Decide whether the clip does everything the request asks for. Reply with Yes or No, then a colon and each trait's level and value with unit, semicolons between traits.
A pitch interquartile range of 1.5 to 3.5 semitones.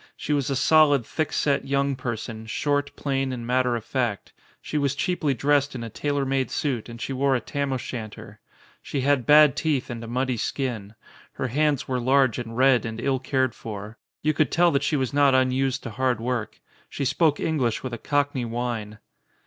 Yes: average, 2.9 semitones